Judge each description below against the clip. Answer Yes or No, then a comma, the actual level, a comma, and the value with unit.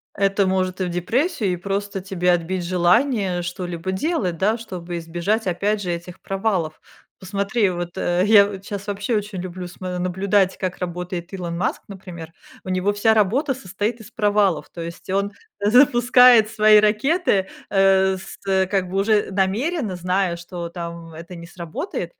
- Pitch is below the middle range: No, high, 190 Hz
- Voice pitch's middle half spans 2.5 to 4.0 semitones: Yes, average, 2.8 semitones